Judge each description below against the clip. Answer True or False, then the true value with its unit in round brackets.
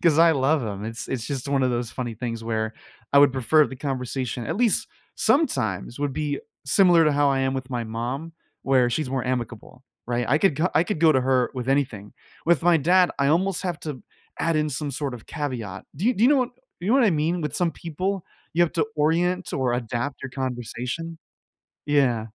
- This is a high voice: False (140 Hz)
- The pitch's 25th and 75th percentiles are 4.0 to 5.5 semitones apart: True (5.0 semitones)